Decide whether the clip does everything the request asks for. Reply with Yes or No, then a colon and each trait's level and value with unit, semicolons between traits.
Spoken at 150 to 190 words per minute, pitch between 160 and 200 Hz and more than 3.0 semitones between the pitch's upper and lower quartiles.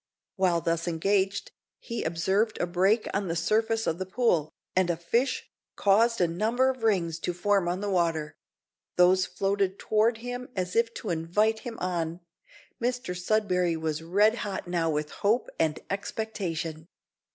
Yes: average, 160 wpm; high, 190 Hz; average, 4.5 semitones